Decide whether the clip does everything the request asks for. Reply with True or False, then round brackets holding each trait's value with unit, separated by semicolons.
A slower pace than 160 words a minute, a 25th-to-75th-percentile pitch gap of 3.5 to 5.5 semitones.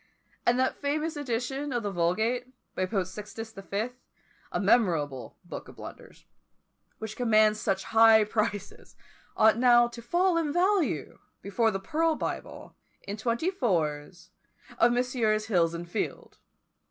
True (140 wpm; 4.2 semitones)